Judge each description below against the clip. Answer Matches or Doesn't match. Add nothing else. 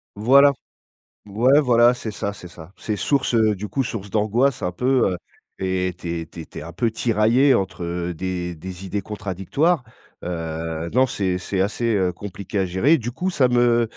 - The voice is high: Doesn't match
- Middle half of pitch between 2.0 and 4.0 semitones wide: Doesn't match